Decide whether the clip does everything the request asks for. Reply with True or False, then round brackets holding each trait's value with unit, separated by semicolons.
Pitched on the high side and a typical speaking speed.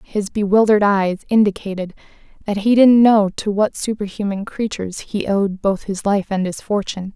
True (205 Hz; 170 wpm)